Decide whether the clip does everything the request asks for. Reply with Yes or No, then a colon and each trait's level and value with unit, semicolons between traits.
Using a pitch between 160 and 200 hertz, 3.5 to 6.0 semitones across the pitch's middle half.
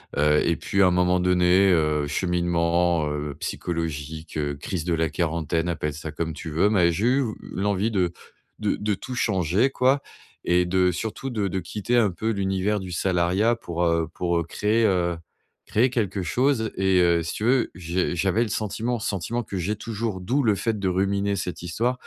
No: very low, 90 Hz; average, 4.0 semitones